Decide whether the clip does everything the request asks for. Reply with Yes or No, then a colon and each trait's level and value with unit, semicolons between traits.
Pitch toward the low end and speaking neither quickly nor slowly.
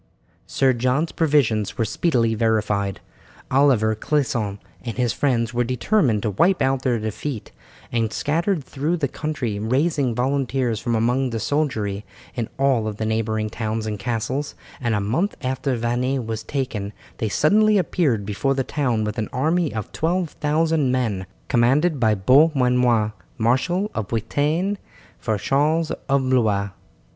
Yes: low, 125 Hz; average, 145 wpm